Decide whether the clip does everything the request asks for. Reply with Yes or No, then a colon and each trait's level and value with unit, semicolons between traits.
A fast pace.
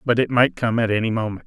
Yes: fast, 285 wpm